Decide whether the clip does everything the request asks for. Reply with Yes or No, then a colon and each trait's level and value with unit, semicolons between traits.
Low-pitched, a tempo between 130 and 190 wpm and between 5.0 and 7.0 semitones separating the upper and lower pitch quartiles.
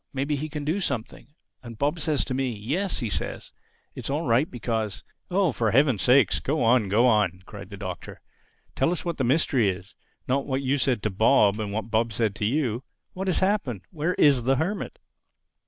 No: low, 130 Hz; average, 200 wpm; average, 5.3 semitones